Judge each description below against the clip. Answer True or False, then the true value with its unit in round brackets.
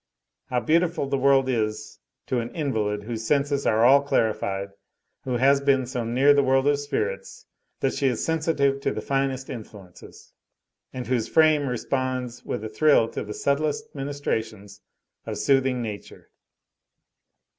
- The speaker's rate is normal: True (150 wpm)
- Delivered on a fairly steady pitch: False (3.7 semitones)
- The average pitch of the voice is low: True (130 Hz)